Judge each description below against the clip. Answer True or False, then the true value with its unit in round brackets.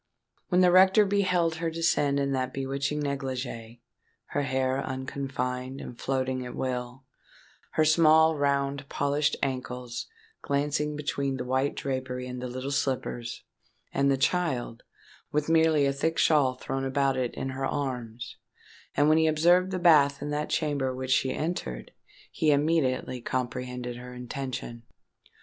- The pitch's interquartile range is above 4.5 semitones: False (2.8 semitones)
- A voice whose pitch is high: False (135 Hz)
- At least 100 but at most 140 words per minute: True (135 wpm)